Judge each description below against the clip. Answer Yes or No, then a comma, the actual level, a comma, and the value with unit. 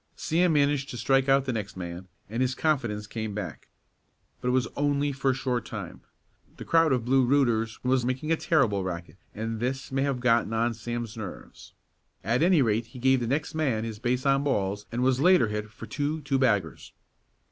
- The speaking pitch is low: Yes, low, 125 Hz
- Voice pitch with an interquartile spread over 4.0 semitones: No, average, 3.7 semitones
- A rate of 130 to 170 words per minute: No, average, 200 wpm